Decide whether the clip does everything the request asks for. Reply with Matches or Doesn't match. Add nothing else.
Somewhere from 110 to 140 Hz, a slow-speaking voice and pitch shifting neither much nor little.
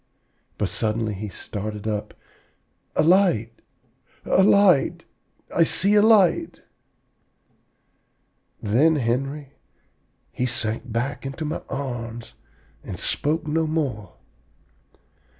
Doesn't match